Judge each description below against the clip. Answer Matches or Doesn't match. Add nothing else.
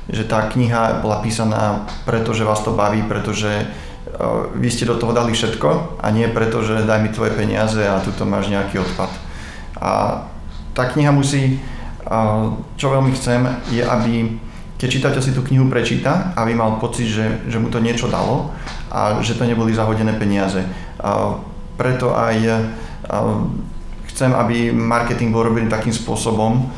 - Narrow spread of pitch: Matches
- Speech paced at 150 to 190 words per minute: Matches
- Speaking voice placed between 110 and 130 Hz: Matches